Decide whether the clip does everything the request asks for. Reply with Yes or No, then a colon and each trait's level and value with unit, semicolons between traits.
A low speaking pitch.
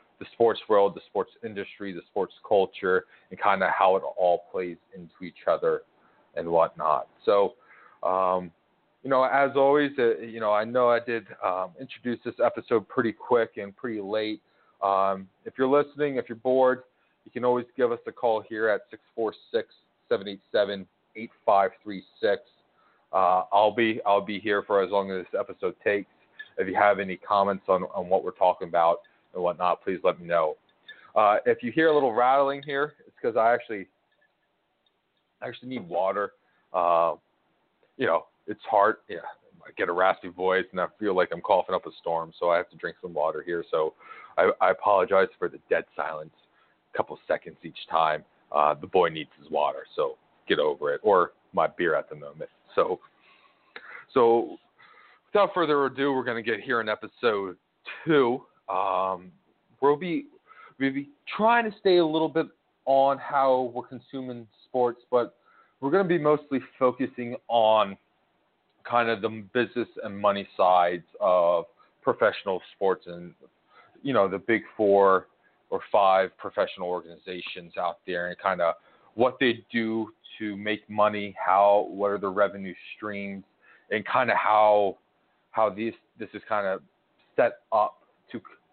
Yes: low, 120 Hz